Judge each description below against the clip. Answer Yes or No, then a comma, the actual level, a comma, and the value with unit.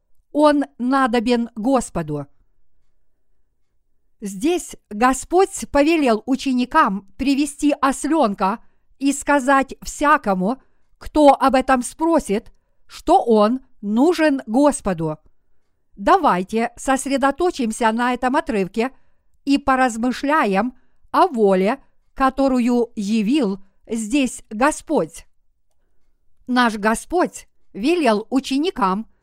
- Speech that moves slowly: Yes, slow, 75 wpm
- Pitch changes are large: No, average, 5.0 semitones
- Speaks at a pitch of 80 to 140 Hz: No, very high, 255 Hz